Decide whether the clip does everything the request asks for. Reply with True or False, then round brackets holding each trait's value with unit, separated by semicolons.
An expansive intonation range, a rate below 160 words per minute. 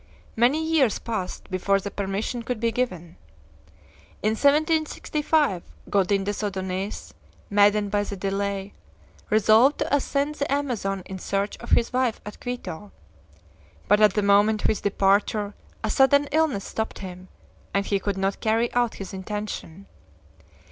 False (3.8 semitones; 145 wpm)